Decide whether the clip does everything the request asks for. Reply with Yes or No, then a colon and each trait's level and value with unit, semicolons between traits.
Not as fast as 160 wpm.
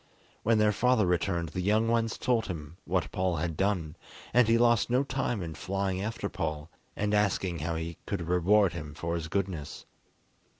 No: average, 180 wpm